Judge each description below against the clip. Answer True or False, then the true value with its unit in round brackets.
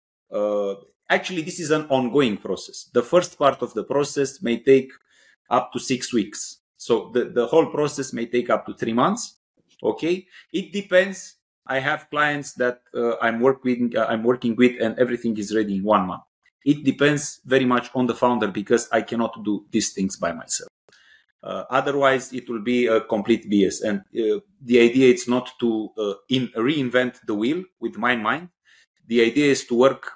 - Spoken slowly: False (185 wpm)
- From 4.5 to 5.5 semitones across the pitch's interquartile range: False (3.5 semitones)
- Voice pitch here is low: True (125 Hz)